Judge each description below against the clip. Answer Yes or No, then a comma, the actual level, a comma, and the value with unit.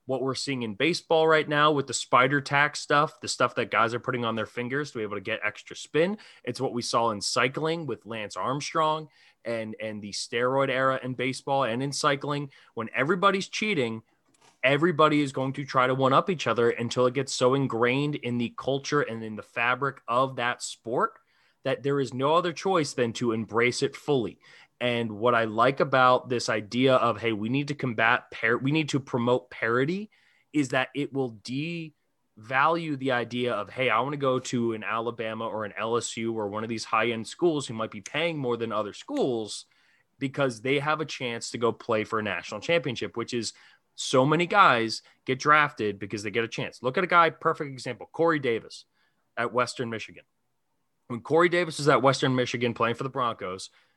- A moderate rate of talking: No, fast, 210 wpm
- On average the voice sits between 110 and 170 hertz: Yes, low, 130 Hz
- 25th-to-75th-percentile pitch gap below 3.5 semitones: No, average, 4.1 semitones